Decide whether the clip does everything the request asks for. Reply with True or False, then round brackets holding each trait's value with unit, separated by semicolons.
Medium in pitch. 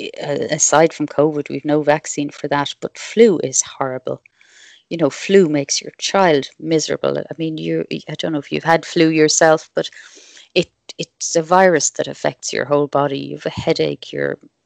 True (150 Hz)